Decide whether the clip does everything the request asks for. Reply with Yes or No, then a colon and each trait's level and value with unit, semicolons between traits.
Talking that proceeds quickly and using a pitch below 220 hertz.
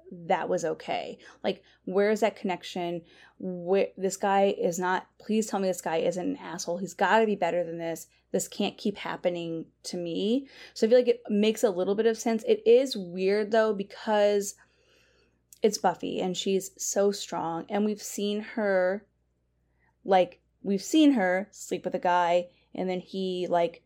No: average, 180 wpm; high, 190 Hz